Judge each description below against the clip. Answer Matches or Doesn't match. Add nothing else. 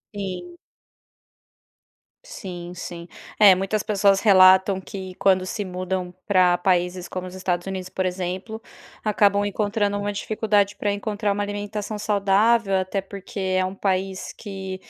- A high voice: Matches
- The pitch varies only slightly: Matches